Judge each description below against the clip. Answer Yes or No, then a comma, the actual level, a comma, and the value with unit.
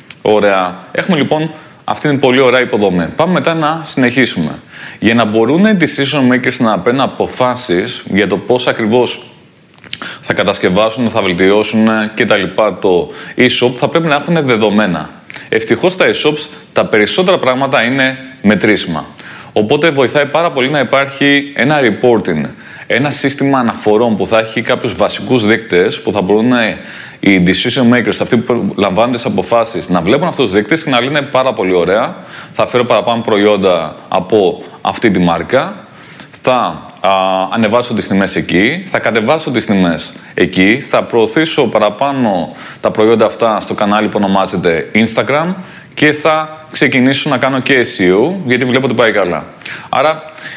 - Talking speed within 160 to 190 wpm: No, average, 150 wpm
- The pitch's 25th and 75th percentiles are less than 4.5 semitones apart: No, average, 5.3 semitones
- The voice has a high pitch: No, low, 125 Hz